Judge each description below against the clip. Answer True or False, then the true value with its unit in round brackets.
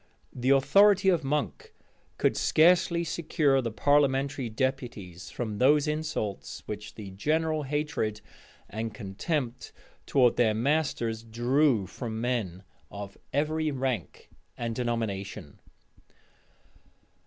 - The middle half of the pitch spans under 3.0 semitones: False (5.5 semitones)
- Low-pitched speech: True (130 Hz)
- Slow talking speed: True (105 wpm)